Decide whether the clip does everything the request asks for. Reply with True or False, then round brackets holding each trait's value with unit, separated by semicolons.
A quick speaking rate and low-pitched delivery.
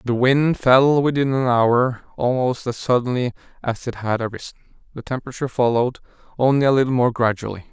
False (165 wpm; 125 Hz)